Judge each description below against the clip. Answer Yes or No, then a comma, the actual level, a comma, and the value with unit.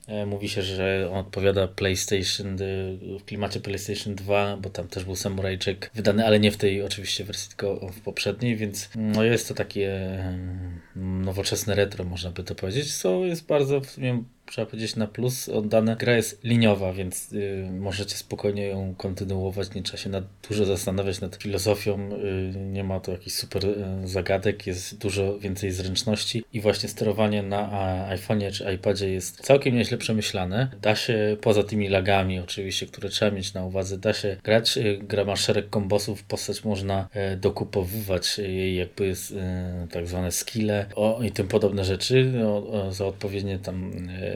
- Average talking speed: No, fast, 170 wpm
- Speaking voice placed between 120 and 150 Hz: No, low, 100 Hz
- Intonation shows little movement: Yes, narrow, 1.7 semitones